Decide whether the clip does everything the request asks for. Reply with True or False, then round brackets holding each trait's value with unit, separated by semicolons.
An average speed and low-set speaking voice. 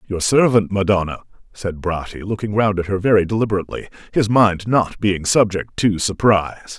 True (160 wpm; 100 Hz)